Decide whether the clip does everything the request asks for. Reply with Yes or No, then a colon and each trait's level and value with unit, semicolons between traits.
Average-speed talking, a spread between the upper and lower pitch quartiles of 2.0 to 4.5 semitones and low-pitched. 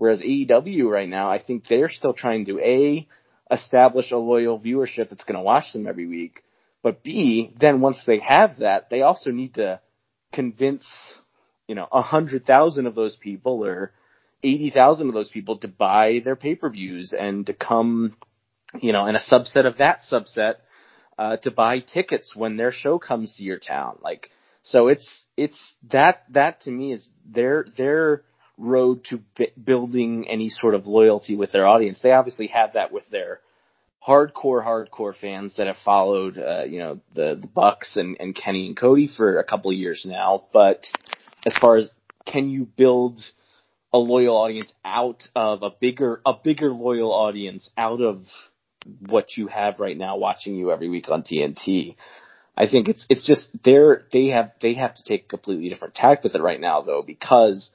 Yes: average, 185 wpm; average, 3.8 semitones; low, 120 Hz